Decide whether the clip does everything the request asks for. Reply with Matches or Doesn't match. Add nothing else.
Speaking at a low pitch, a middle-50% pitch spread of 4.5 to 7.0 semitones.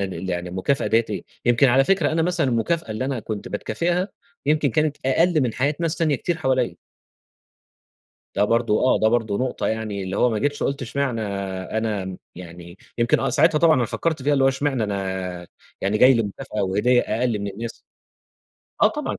Matches